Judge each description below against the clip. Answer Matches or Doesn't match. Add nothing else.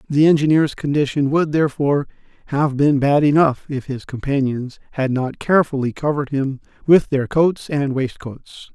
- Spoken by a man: Matches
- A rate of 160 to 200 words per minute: Doesn't match